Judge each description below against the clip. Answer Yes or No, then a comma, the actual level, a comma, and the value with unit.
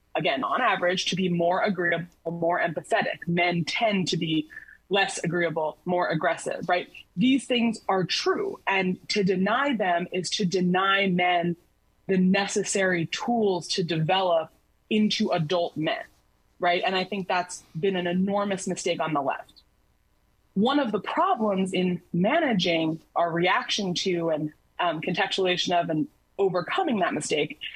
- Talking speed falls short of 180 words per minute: Yes, average, 145 wpm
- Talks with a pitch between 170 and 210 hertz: Yes, medium, 185 Hz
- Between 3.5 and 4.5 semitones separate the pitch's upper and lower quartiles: No, average, 2.7 semitones